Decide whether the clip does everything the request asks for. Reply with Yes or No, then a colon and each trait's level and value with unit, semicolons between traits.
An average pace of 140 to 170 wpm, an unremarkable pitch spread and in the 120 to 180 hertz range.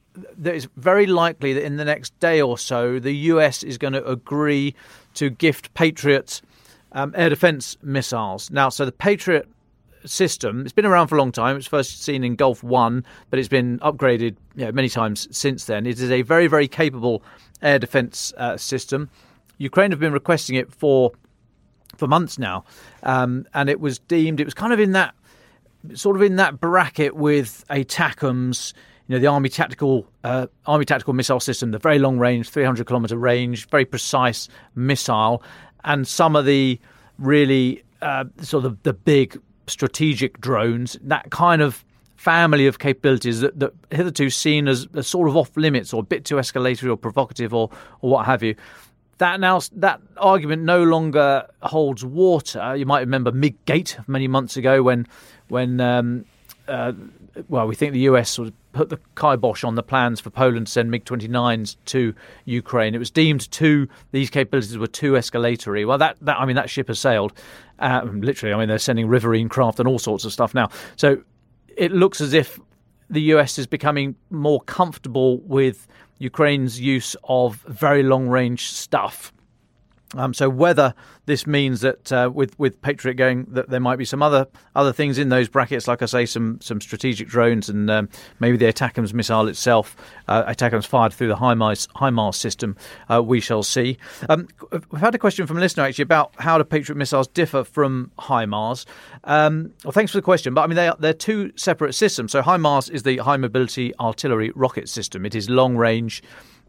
No: average, 185 wpm; average, 3.5 semitones; low, 135 Hz